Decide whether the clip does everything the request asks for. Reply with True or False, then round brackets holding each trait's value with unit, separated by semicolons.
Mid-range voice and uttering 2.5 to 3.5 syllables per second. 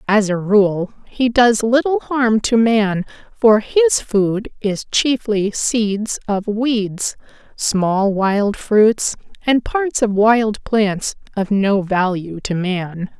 False (215 Hz; 2.9 syllables/s)